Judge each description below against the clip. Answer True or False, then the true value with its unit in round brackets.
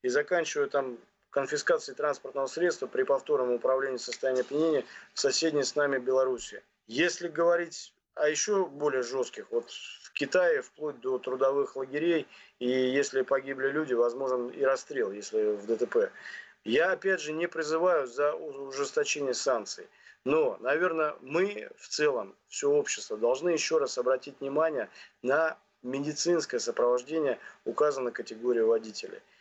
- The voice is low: False (165 Hz)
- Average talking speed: True (135 wpm)